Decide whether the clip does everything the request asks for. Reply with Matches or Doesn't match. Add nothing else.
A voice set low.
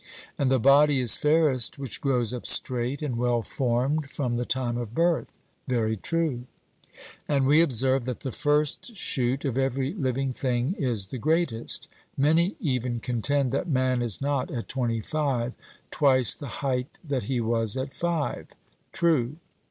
Matches